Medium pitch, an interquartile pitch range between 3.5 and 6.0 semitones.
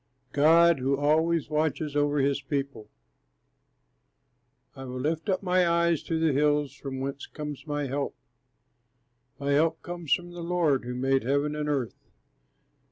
No: medium, 145 Hz; average, 2.9 semitones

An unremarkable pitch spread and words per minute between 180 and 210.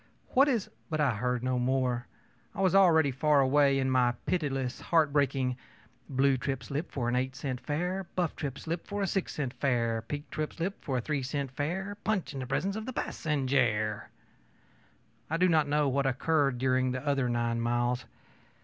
Yes: average, 3.9 semitones; average, 190 wpm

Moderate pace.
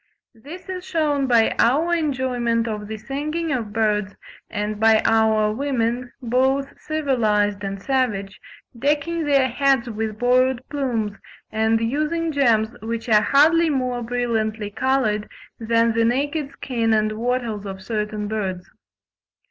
No: slow, 130 wpm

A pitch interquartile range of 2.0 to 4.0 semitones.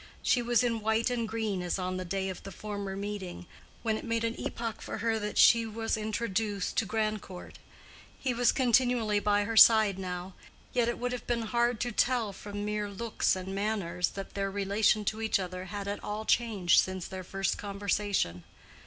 Yes: average, 2.8 semitones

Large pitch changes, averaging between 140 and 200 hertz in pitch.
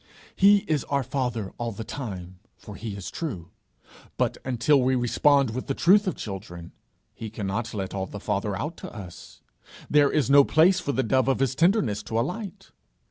No: wide, 6.1 semitones; low, 125 Hz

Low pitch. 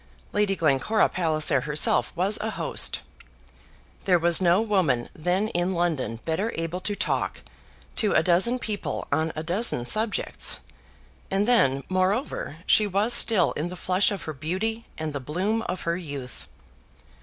No: medium, 180 Hz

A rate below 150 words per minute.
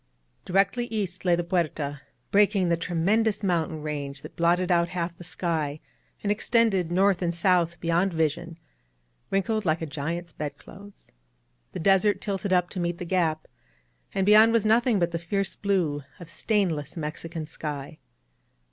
No: average, 160 wpm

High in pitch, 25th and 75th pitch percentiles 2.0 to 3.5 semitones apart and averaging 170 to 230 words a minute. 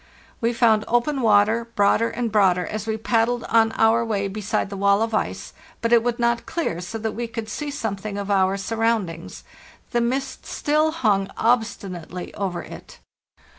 Yes: high, 225 Hz; average, 2.9 semitones; average, 175 wpm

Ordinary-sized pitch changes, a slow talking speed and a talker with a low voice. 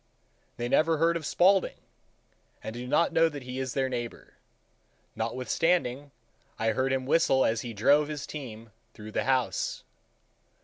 No: average, 4.1 semitones; average, 145 wpm; low, 130 Hz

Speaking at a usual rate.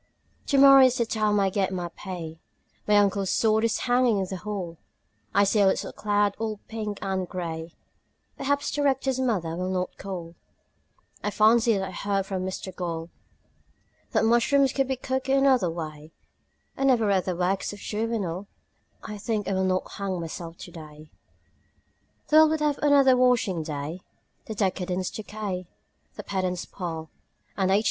Yes: average, 165 wpm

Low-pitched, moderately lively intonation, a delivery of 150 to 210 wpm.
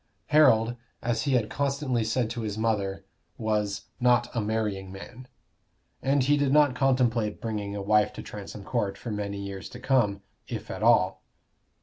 Yes: low, 110 Hz; average, 3.5 semitones; average, 160 wpm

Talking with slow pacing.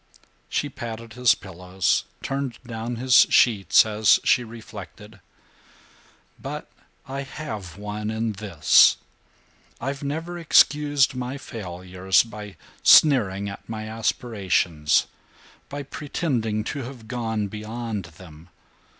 Yes: slow, 105 wpm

